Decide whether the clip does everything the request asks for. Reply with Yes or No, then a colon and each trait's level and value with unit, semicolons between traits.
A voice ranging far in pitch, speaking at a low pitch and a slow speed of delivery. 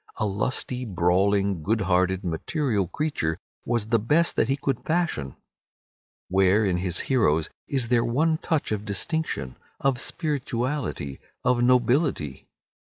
Yes: wide, 6.5 semitones; low, 115 Hz; slow, 130 wpm